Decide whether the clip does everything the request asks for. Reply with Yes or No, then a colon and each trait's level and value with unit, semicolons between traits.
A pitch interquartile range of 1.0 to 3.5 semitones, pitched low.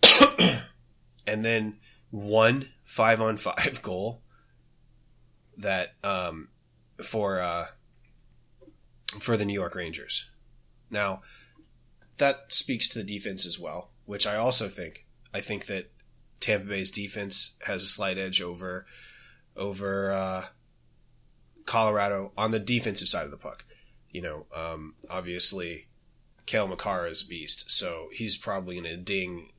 Yes: average, 3.2 semitones; low, 100 Hz